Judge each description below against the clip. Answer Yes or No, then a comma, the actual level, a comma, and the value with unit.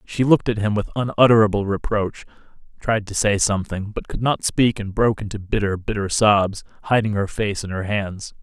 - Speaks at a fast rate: No, average, 190 wpm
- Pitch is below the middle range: Yes, low, 105 Hz